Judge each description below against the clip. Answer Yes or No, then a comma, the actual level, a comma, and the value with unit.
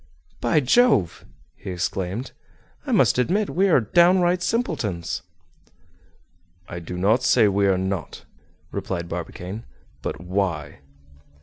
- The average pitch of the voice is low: Yes, low, 100 Hz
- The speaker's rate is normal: No, slow, 120 wpm